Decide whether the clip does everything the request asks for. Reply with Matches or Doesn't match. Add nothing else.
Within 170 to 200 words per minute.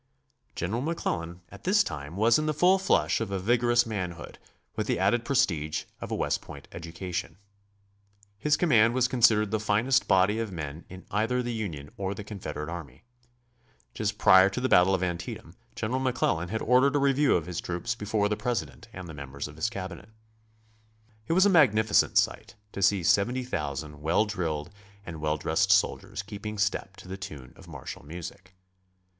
Matches